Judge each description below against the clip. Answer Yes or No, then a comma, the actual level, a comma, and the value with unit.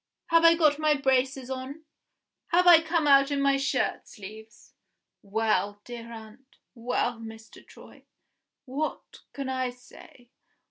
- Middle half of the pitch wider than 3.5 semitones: Yes, average, 4.0 semitones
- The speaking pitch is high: Yes, very high, 260 Hz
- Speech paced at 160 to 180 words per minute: No, slow, 135 wpm